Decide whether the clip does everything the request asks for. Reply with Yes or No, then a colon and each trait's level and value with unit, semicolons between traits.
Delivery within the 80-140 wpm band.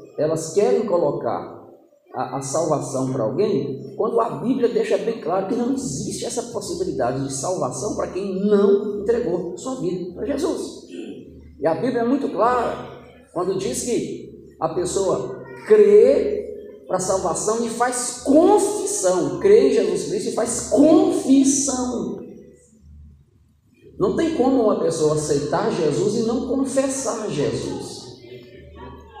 Yes: average, 135 wpm